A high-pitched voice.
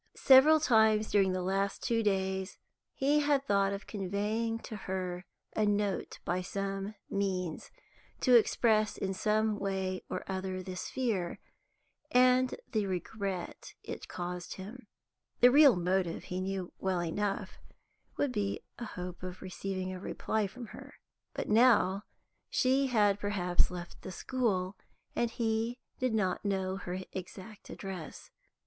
Yes: high, 200 Hz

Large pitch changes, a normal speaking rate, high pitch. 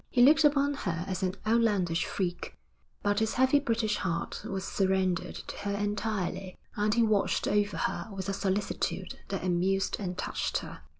No: average, 3.0 semitones; average, 170 wpm; high, 200 Hz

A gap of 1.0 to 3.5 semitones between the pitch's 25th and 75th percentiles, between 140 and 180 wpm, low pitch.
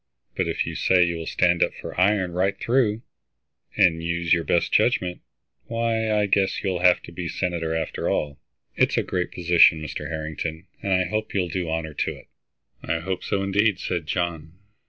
No: average, 2.9 semitones; average, 190 wpm; very low, 90 Hz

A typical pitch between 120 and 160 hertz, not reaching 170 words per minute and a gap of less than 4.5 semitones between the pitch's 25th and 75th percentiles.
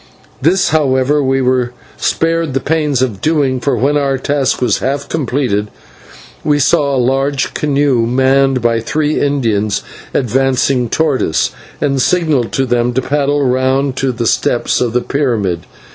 Yes: low, 135 Hz; average, 155 wpm; average, 2.7 semitones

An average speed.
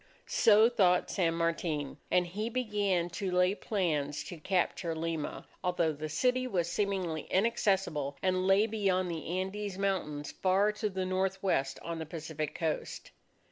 Yes: average, 145 wpm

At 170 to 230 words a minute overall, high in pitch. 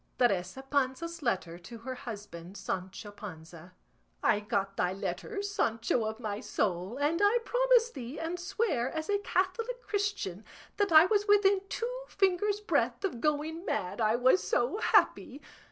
No: average, 155 wpm; very high, 270 Hz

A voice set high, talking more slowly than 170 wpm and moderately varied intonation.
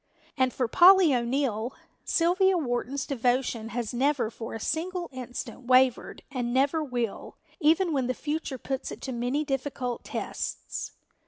Yes: very high, 260 Hz; average, 145 wpm; average, 3.7 semitones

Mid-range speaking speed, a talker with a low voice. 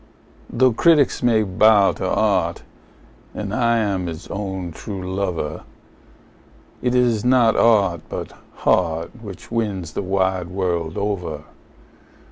No: slow, 120 wpm; low, 100 Hz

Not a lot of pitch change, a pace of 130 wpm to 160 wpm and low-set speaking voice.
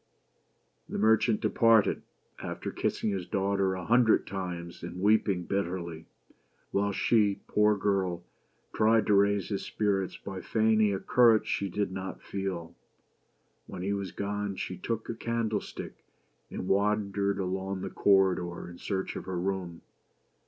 Yes: narrow, 2.0 semitones; average, 145 wpm; low, 100 Hz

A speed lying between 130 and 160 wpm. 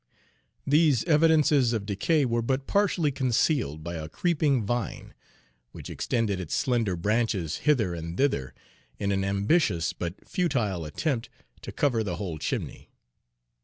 Yes: average, 145 wpm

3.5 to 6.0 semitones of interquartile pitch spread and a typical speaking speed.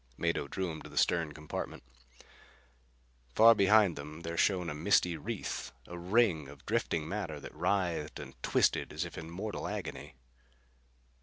Yes: average, 3.8 semitones; average, 155 wpm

